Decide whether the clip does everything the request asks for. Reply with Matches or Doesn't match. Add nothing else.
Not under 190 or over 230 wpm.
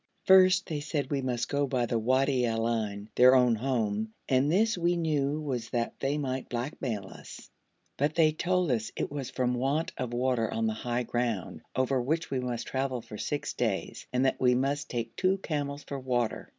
Matches